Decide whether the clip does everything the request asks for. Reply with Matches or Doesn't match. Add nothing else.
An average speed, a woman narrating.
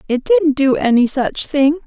Matches